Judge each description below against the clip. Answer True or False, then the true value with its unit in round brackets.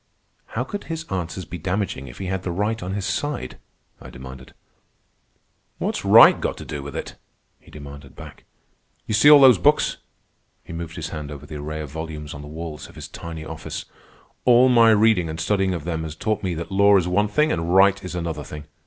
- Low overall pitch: True (85 Hz)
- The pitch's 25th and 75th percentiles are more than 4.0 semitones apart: True (4.8 semitones)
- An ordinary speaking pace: False (215 wpm)